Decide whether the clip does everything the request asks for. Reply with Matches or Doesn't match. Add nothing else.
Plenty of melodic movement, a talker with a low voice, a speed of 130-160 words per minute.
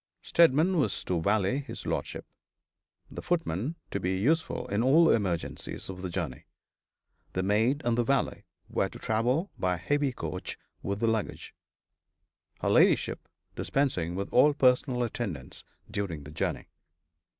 Matches